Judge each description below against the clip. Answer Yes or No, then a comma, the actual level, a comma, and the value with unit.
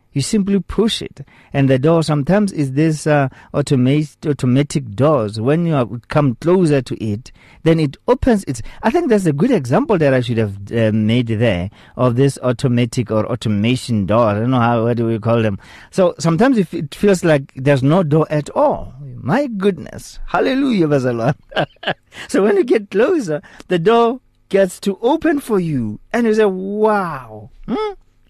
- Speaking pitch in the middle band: Yes, medium, 145 Hz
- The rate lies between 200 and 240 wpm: No, average, 170 wpm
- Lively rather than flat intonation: Yes, wide, 8.1 semitones